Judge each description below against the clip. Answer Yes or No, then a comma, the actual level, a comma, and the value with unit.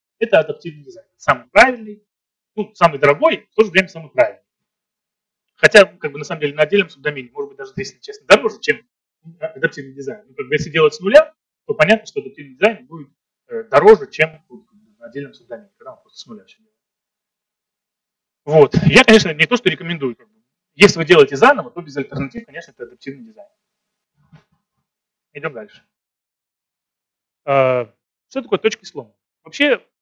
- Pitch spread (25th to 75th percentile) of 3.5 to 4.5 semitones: No, average, 4.9 semitones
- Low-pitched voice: No, high, 210 Hz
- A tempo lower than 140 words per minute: No, fast, 160 wpm